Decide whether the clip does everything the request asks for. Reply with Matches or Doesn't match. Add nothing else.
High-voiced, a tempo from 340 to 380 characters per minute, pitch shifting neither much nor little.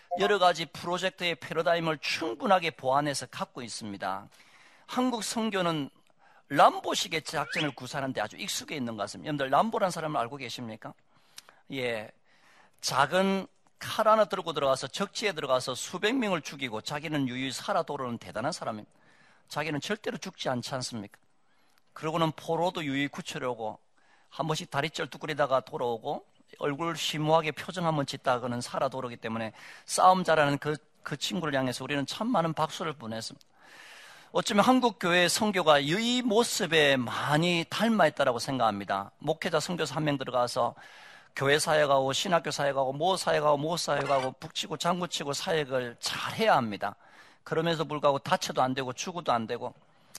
Doesn't match